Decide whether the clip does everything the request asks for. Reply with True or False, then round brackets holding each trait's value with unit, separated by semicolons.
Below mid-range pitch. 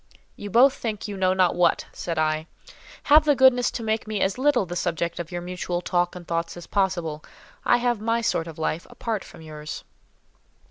False (185 Hz)